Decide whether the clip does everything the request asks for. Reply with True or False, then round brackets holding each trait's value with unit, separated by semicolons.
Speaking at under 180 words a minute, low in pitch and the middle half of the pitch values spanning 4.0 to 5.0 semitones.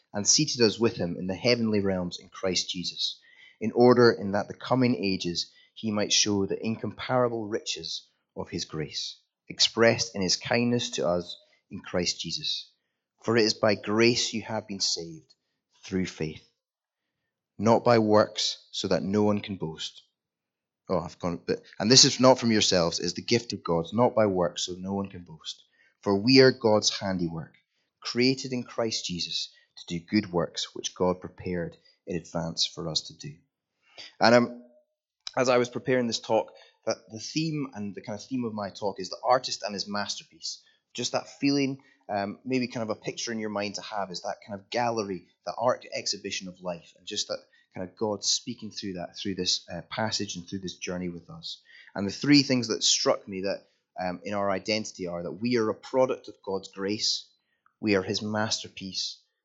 False (200 wpm; 105 Hz; 4.4 semitones)